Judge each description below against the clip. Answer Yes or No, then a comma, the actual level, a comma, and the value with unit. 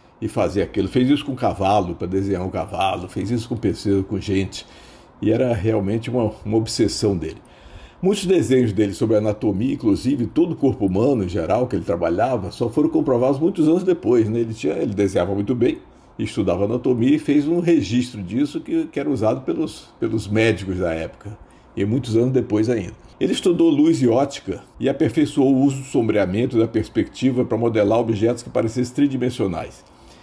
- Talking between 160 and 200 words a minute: Yes, fast, 185 wpm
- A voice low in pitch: Yes, low, 115 Hz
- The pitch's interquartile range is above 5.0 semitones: Yes, wide, 5.6 semitones